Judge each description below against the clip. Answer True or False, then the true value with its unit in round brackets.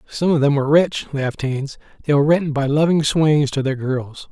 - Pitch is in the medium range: True (145 Hz)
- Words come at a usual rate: False (220 wpm)